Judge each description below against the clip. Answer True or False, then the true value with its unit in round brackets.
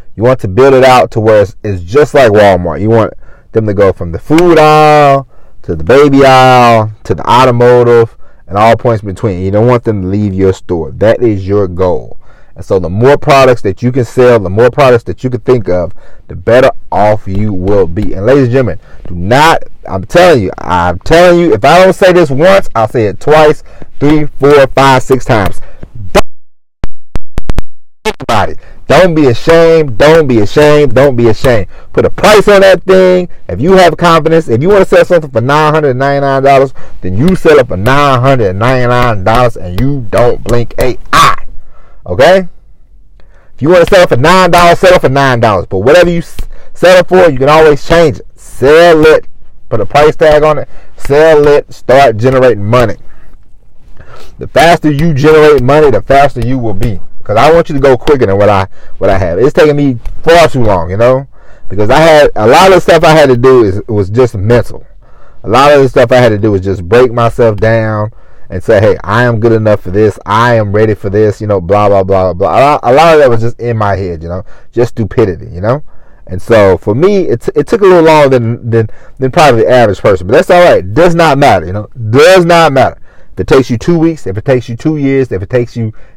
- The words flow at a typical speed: False (220 wpm)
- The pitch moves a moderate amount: False (5.7 semitones)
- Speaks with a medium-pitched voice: False (125 Hz)